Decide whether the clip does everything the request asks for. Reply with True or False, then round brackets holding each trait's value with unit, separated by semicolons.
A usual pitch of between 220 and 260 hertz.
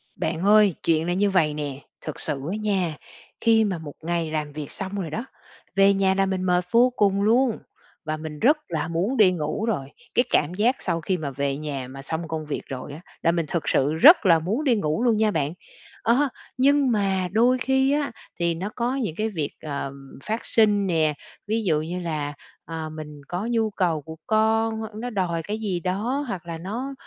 False (185 Hz)